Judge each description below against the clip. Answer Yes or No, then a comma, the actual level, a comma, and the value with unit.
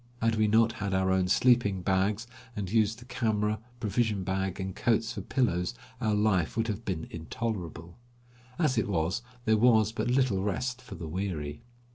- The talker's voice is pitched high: No, low, 105 Hz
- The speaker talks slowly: No, average, 175 wpm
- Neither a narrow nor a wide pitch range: Yes, average, 3.4 semitones